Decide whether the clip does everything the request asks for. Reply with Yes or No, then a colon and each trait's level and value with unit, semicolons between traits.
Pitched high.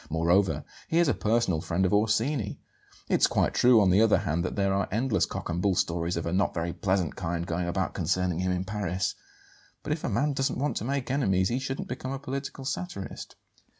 No: low, 100 Hz